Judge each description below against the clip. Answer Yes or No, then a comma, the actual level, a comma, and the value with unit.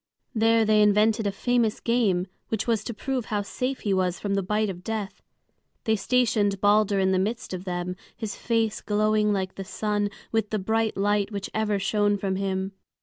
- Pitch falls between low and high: No, high, 210 Hz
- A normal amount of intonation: No, narrow, 2.1 semitones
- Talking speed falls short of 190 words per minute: No, average, 195 wpm